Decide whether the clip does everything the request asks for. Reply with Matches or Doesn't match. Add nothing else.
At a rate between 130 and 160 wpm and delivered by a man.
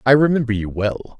Doesn't match